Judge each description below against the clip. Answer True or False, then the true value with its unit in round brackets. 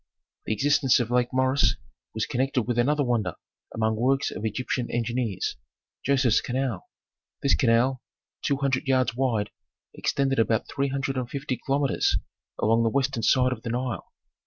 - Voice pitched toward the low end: True (125 Hz)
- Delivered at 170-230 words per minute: False (155 wpm)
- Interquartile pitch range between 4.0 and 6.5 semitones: False (2.8 semitones)